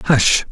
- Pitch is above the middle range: No, low, 130 Hz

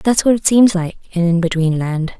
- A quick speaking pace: Yes, fast, 245 wpm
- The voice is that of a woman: Yes, female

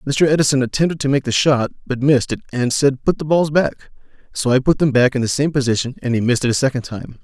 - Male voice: Yes, male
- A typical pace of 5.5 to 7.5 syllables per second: Yes, 6.5 syllables/s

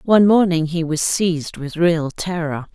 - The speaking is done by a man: No, female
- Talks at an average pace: Yes, average, 175 wpm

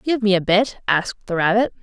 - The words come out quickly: Yes, fast, 230 wpm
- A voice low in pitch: No, high, 205 Hz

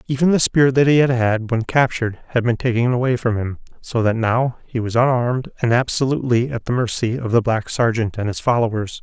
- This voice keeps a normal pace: No, fast, 220 wpm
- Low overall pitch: Yes, low, 120 Hz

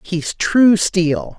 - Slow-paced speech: Yes, slow, 130 wpm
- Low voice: No, high, 190 Hz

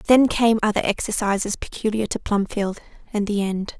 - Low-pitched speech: No, high, 210 Hz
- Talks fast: No, average, 160 wpm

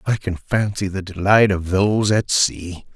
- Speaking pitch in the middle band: No, very low, 95 Hz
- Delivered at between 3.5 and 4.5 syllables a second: Yes, 4.4 syllables/s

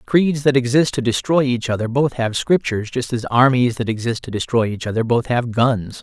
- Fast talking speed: Yes, fast, 220 wpm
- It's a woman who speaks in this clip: No, male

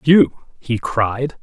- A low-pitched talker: Yes, low, 125 Hz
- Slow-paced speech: Yes, slow, 125 wpm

